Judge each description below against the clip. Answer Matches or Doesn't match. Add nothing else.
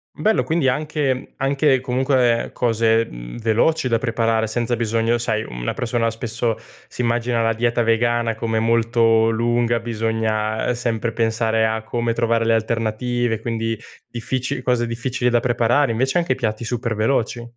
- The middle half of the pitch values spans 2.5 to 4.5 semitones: Doesn't match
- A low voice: Matches